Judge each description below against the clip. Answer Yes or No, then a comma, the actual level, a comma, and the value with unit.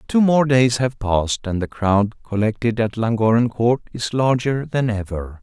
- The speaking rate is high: No, average, 175 wpm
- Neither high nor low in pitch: No, low, 115 Hz